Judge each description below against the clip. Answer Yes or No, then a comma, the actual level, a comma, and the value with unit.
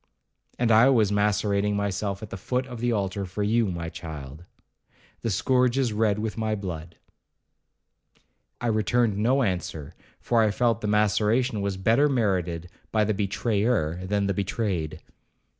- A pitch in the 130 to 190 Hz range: No, low, 105 Hz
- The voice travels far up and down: No, average, 3.3 semitones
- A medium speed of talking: Yes, average, 150 wpm